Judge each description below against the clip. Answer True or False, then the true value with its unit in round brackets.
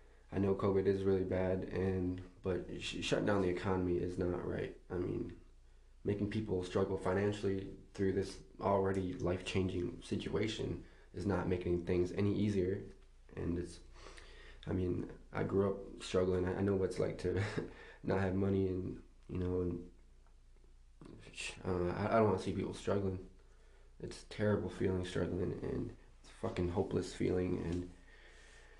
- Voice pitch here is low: True (95 Hz)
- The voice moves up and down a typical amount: False (1.6 semitones)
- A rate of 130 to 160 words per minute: True (155 wpm)